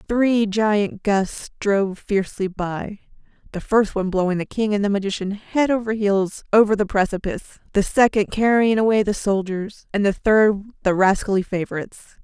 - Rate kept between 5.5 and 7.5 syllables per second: No, 5.1 syllables/s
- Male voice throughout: No, female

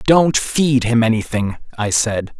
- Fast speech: No, average, 150 wpm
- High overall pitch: No, low, 120 Hz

